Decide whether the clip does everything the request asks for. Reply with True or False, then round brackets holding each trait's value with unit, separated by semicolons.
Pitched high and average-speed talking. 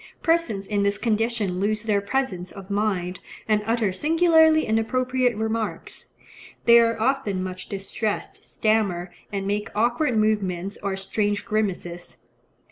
False (215 Hz; 125 wpm)